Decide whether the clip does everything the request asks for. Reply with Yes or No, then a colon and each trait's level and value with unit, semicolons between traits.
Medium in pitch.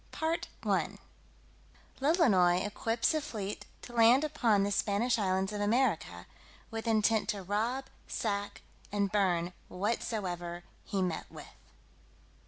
No: high, 210 Hz